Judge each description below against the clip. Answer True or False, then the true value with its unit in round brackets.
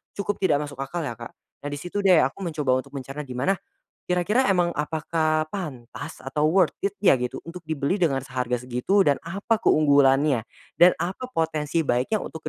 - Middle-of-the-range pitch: True (155 Hz)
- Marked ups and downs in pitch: False (4.7 semitones)